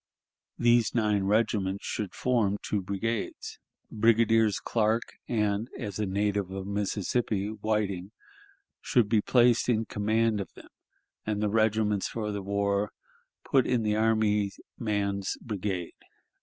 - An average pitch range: No, narrow, 1.9 semitones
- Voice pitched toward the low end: Yes, low, 105 Hz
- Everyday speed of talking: No, slow, 130 wpm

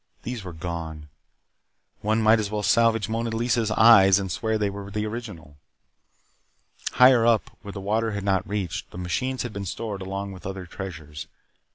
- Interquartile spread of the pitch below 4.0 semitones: Yes, average, 3.0 semitones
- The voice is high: No, low, 100 Hz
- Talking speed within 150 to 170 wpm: No, average, 180 wpm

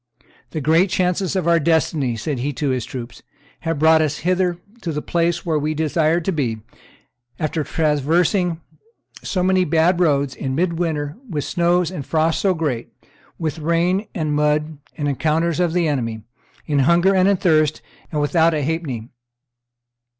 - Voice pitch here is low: No, medium, 160 Hz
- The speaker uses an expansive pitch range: No, average, 2.8 semitones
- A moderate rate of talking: Yes, average, 160 wpm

